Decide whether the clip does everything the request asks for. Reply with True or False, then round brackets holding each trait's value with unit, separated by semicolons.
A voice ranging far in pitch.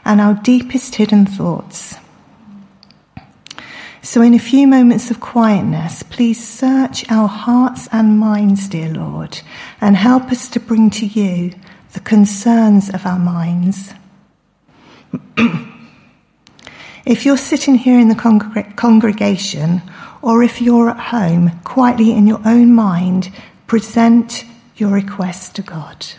False (3.3 semitones)